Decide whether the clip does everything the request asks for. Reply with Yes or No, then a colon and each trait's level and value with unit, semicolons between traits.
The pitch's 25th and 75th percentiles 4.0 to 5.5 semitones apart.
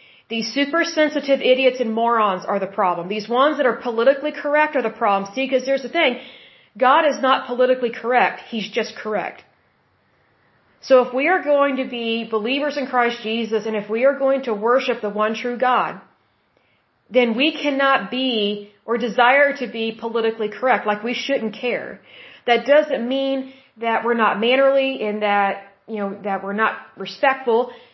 No: average, 3.5 semitones